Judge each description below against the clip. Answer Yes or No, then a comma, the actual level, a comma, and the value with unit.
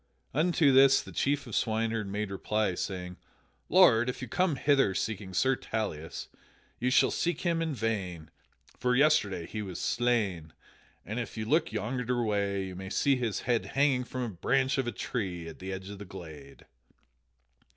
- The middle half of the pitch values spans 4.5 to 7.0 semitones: Yes, wide, 5.6 semitones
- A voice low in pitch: Yes, low, 110 Hz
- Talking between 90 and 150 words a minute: No, average, 170 wpm